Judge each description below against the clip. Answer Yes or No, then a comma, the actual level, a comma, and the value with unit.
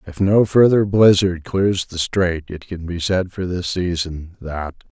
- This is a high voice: No, very low, 90 Hz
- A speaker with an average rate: Yes, average, 180 wpm